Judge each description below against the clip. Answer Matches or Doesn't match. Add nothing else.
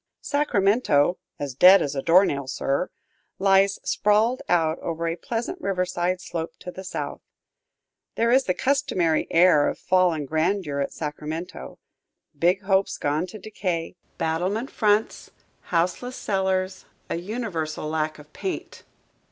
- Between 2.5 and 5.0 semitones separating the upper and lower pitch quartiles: Matches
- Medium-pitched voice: Matches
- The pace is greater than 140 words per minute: Doesn't match